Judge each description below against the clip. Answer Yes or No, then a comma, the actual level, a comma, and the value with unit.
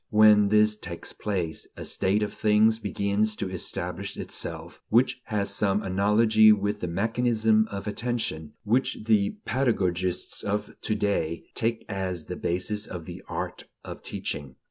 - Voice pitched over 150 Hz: No, low, 105 Hz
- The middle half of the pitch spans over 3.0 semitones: No, narrow, 2.5 semitones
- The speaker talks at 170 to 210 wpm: No, average, 145 wpm